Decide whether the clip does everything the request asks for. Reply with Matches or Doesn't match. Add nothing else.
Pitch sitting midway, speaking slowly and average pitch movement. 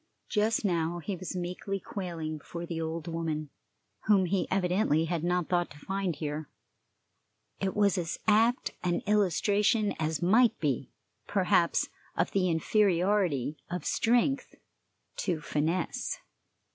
Matches